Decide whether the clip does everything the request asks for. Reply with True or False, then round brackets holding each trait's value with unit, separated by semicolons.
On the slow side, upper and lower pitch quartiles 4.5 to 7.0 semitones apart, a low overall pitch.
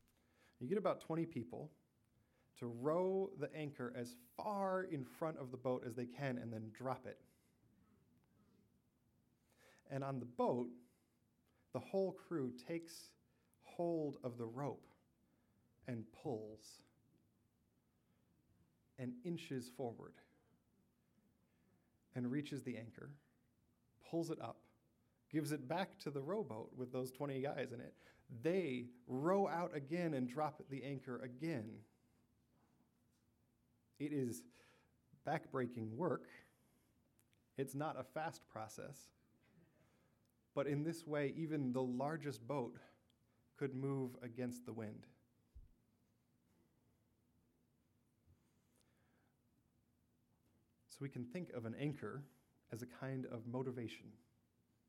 False (110 wpm; 3.8 semitones; 130 Hz)